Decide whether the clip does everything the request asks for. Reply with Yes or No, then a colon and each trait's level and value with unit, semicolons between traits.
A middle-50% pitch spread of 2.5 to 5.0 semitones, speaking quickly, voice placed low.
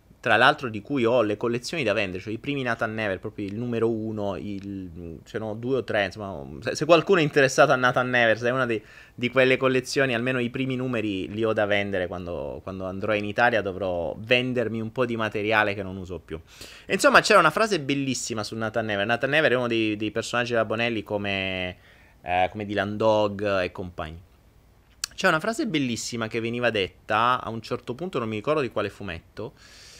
Yes: average, 3.7 semitones; fast, 205 wpm; low, 110 Hz